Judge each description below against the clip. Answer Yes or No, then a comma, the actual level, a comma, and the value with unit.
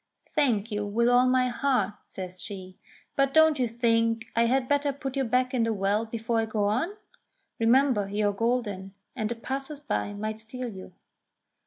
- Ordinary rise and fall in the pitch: Yes, average, 3.6 semitones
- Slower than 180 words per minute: No, average, 185 wpm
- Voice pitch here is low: No, high, 230 Hz